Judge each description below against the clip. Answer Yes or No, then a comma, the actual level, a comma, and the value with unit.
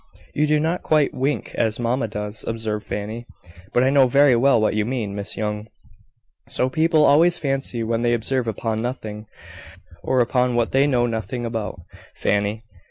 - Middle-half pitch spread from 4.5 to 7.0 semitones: No, average, 3.7 semitones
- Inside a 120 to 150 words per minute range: No, average, 170 wpm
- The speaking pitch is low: Yes, low, 120 Hz